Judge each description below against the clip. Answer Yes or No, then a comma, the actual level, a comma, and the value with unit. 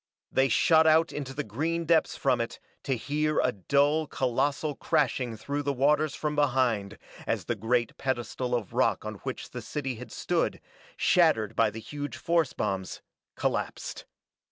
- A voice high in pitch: No, low, 135 Hz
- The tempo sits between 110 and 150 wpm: No, average, 160 wpm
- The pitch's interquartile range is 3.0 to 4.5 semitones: Yes, average, 3.9 semitones